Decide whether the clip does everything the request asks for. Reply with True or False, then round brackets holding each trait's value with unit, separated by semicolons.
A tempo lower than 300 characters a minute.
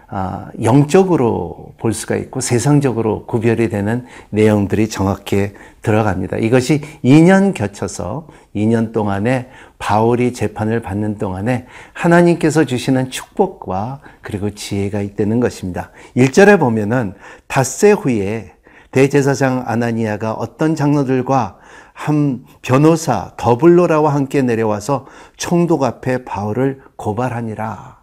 True (275 characters per minute)